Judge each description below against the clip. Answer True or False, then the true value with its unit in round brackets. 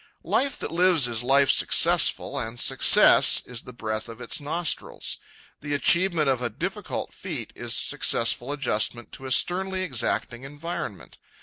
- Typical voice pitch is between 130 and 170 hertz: True (135 Hz)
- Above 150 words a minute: False (145 wpm)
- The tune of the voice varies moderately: False (5.7 semitones)